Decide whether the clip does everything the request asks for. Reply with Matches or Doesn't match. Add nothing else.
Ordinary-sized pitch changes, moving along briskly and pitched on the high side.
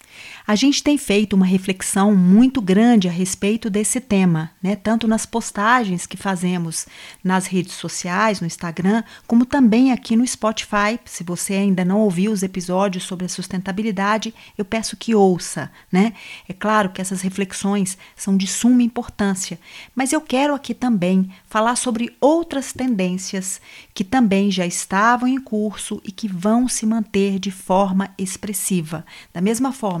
Doesn't match